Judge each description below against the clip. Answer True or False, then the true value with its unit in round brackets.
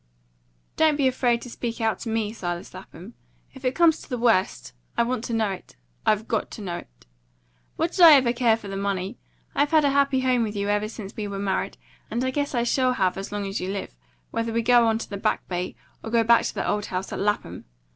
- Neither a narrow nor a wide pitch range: True (4.0 semitones)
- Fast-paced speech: True (245 wpm)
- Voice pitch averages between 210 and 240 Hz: True (225 Hz)